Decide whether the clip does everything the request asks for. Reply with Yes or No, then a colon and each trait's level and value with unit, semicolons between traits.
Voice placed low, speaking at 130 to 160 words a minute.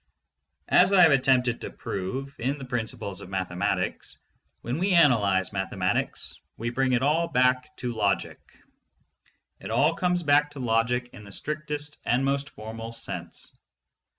Yes: low, 125 Hz; average, 150 wpm